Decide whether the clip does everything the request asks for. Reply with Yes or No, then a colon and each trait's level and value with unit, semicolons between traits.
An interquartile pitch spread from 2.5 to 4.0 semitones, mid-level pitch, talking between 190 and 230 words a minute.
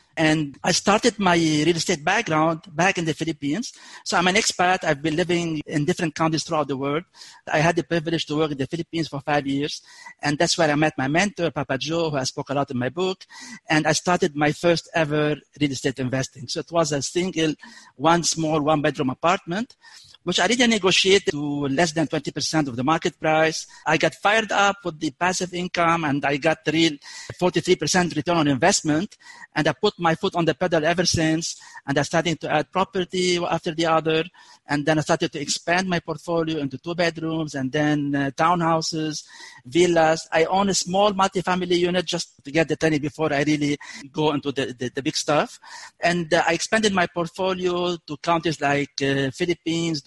Yes: average, 2.9 semitones; medium, 165 Hz; average, 200 wpm